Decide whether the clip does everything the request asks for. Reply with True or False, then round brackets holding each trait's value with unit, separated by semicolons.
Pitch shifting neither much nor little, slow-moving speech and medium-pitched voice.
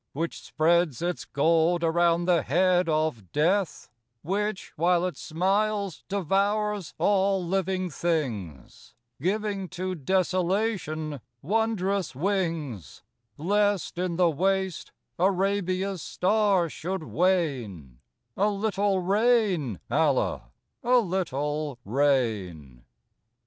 True (4.2 semitones; 95 wpm; 180 Hz)